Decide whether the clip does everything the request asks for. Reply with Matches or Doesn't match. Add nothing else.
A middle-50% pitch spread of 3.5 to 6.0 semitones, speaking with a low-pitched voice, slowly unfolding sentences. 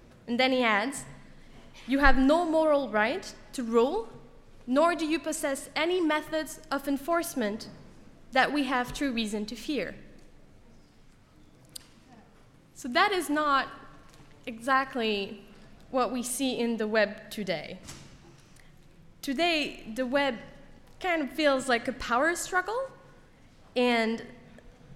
Doesn't match